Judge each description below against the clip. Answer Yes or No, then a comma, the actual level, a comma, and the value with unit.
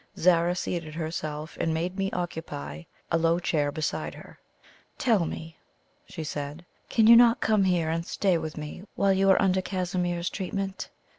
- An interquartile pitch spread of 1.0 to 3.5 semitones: Yes, average, 3.1 semitones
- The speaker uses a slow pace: No, average, 165 wpm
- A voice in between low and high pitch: Yes, medium, 175 Hz